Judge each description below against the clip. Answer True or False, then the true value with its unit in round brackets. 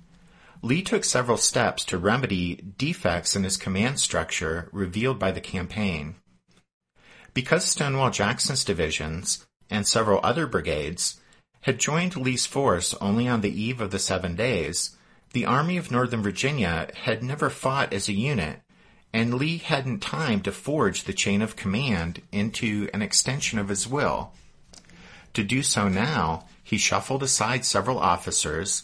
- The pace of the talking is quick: False (150 wpm)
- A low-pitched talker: True (110 Hz)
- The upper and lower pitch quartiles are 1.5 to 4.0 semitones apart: False (5.3 semitones)